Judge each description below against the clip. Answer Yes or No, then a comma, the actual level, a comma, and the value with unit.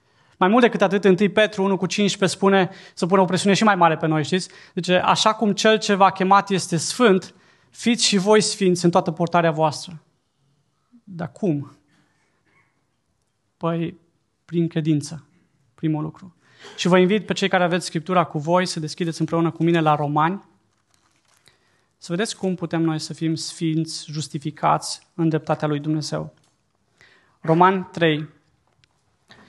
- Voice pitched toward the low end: No, medium, 165 Hz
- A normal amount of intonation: Yes, average, 3.5 semitones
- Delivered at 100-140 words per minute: No, average, 155 wpm